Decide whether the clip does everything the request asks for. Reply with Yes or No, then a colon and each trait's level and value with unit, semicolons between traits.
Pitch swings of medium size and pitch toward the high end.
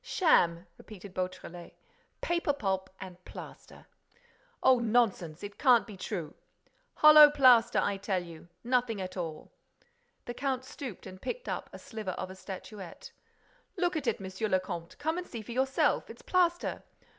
No: wide, 5.9 semitones; high, 210 Hz